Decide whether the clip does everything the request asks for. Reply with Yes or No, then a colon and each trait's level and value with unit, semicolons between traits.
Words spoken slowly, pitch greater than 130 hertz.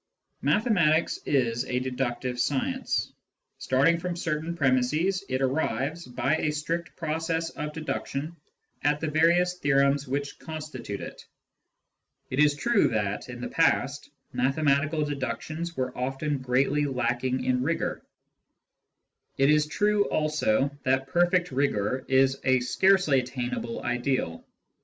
Yes: slow, 125 wpm; medium, 140 Hz